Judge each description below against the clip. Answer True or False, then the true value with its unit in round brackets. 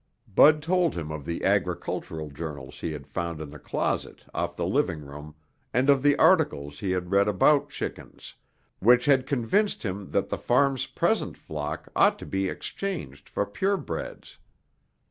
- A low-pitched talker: True (95 Hz)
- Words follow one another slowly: False (165 wpm)